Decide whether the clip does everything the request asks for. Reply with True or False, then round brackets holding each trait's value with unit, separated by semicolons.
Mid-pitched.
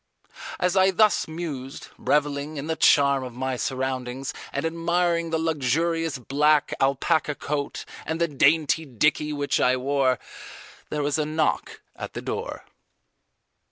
True (150 Hz)